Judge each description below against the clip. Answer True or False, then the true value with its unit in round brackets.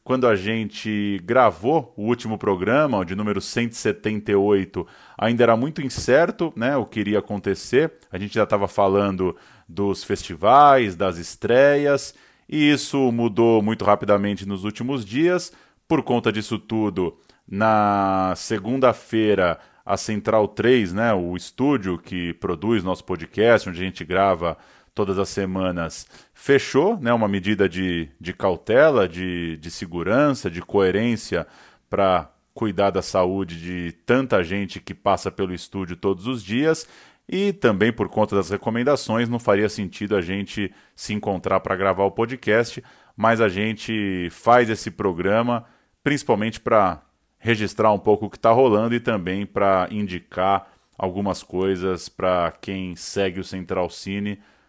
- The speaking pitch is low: True (105 Hz)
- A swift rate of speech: False (140 wpm)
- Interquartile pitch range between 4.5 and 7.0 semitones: False (3.3 semitones)